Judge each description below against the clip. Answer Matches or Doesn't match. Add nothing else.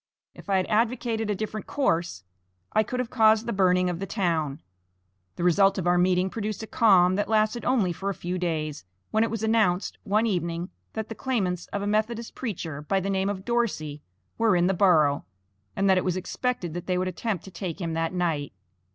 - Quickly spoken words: Matches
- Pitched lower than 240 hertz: Matches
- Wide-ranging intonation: Doesn't match